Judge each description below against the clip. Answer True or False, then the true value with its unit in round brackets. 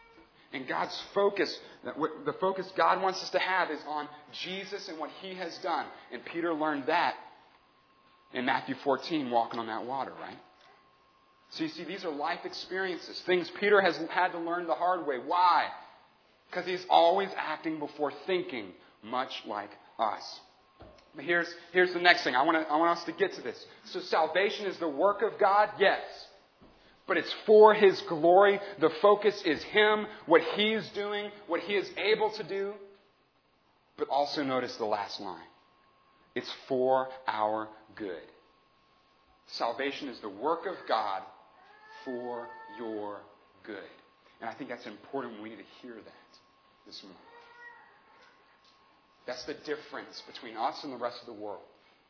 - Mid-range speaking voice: True (180 Hz)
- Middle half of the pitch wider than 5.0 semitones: True (5.5 semitones)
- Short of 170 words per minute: True (160 wpm)